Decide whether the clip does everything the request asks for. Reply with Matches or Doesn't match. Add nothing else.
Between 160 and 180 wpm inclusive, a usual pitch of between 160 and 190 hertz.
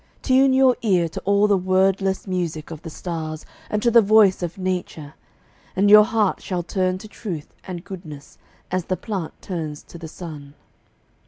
Matches